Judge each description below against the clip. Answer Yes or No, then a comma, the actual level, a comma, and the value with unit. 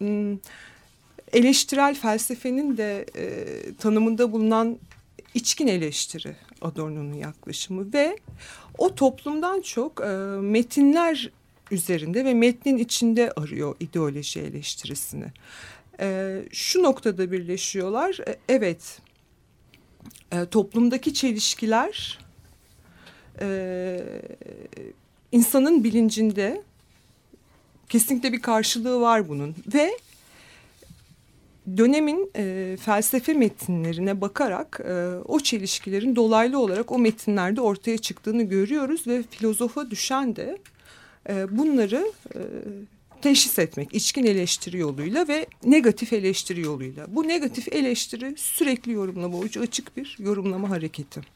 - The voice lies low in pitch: No, high, 225 Hz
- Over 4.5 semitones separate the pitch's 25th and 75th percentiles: Yes, wide, 5.6 semitones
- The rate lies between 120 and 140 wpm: No, slow, 95 wpm